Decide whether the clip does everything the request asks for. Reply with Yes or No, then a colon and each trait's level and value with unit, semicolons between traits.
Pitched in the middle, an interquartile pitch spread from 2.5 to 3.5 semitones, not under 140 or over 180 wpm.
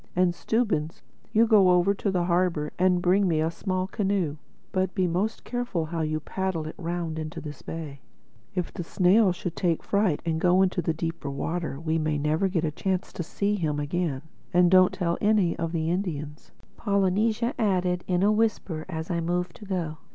No: medium, 175 Hz; average, 2.9 semitones; average, 195 wpm